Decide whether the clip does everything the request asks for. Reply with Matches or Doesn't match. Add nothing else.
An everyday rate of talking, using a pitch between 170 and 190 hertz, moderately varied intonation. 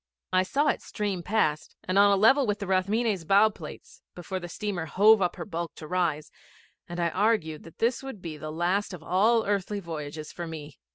Doesn't match